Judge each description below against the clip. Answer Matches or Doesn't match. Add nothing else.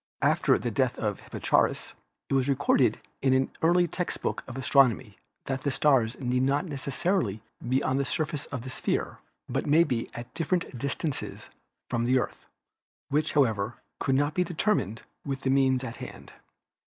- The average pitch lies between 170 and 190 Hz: Doesn't match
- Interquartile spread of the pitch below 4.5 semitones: Matches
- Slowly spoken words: Doesn't match